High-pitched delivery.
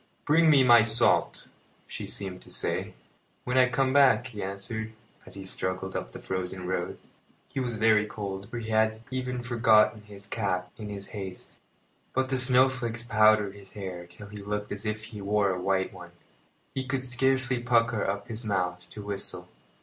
No: low, 110 Hz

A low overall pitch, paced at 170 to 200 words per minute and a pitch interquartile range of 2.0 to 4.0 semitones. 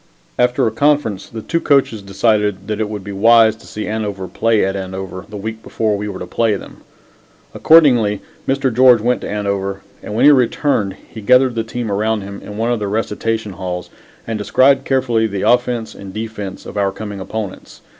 Yes: low, 110 Hz; average, 195 wpm; average, 2.8 semitones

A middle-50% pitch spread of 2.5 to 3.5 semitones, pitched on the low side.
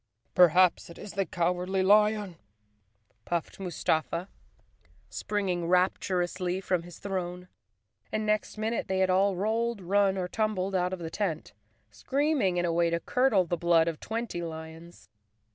No: average, 2.8 semitones; medium, 185 Hz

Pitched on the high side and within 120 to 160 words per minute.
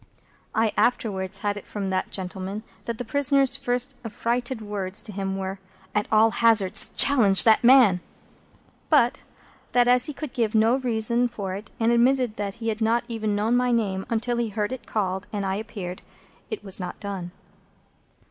No: high, 220 Hz; average, 175 wpm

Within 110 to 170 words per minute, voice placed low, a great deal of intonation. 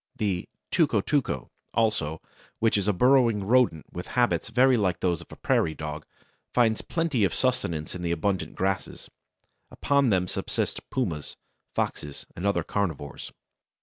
Yes: average, 150 wpm; low, 100 Hz; wide, 6.3 semitones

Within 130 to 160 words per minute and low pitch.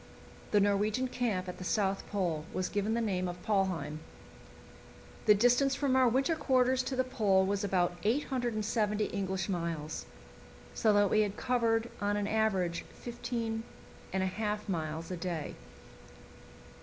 No: average, 145 wpm; high, 205 Hz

